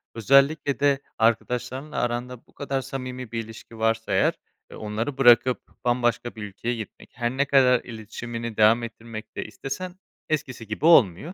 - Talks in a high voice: No, low, 120 Hz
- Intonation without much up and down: No, average, 3.2 semitones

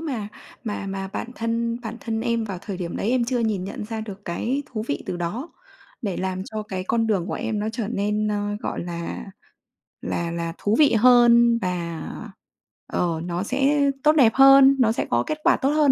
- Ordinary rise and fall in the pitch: Yes, average, 4.0 semitones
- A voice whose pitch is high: Yes, high, 220 Hz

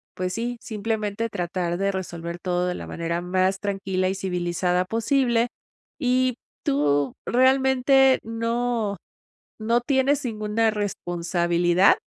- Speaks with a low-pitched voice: No, high, 200 Hz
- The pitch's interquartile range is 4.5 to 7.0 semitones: Yes, average, 5.0 semitones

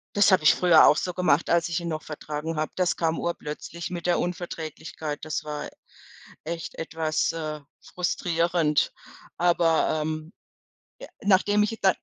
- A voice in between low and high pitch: Yes, medium, 165 Hz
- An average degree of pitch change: No, narrow, 2.2 semitones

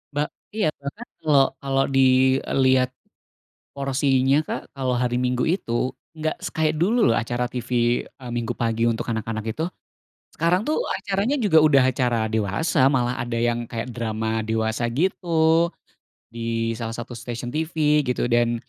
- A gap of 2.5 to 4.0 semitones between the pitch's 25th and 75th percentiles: No, average, 4.7 semitones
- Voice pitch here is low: Yes, low, 125 Hz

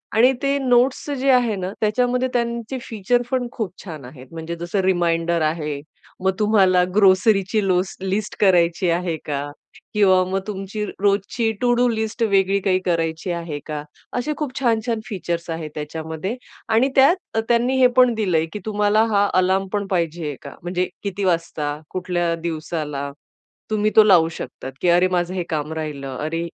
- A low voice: No, high, 190 Hz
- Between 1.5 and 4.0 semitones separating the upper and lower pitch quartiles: No, average, 4.7 semitones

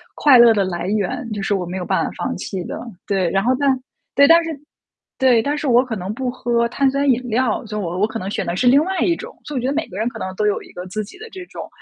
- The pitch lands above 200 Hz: Yes, high, 235 Hz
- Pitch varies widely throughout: Yes, wide, 5.7 semitones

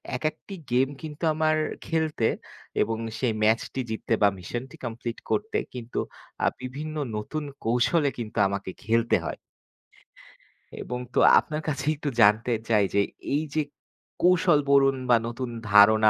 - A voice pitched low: Yes, low, 125 Hz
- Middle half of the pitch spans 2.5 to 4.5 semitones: No, average, 5.3 semitones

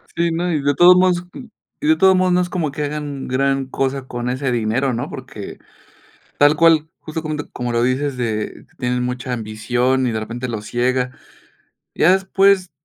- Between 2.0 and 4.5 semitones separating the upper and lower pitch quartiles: No, average, 5.1 semitones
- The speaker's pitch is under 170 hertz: Yes, low, 135 Hz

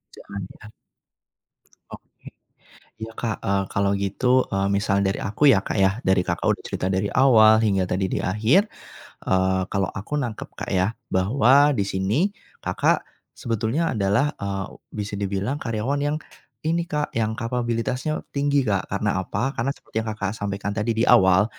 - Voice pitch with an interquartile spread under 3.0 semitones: No, average, 4.3 semitones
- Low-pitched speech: Yes, low, 110 Hz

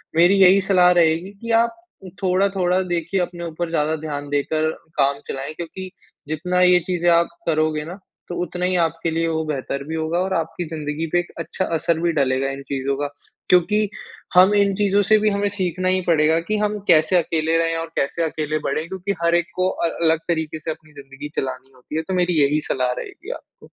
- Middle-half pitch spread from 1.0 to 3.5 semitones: Yes, average, 2.9 semitones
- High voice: No, medium, 165 Hz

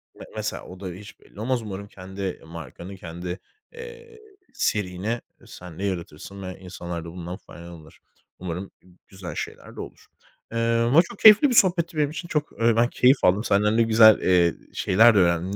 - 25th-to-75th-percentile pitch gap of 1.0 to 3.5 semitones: No, average, 4.9 semitones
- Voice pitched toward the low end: Yes, low, 100 Hz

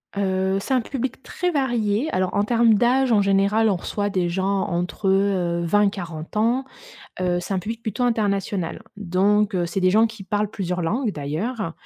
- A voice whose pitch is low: No, high, 200 Hz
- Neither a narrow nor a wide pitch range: Yes, average, 3.4 semitones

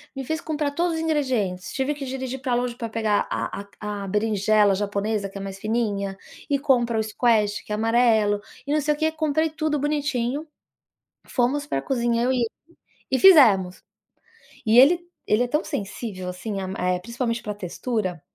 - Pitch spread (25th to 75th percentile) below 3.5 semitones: No, wide, 5.4 semitones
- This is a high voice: Yes, high, 235 Hz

